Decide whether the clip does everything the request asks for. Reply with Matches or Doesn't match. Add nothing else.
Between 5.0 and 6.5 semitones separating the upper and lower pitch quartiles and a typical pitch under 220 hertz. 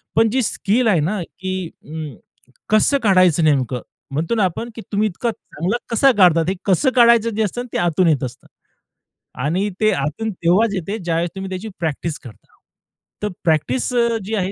Matches